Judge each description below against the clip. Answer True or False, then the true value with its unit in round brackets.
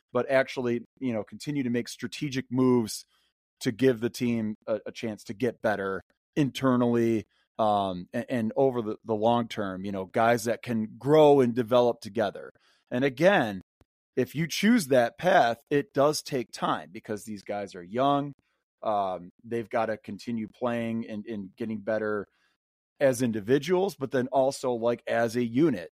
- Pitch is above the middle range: False (120 Hz)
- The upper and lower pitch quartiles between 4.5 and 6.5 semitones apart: False (3.3 semitones)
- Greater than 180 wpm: False (165 wpm)